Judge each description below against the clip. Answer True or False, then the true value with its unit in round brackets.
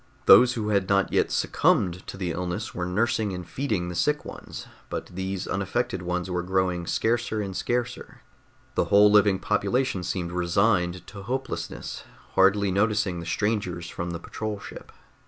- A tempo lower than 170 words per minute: True (160 wpm)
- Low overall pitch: True (95 Hz)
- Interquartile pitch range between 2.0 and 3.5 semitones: True (3.1 semitones)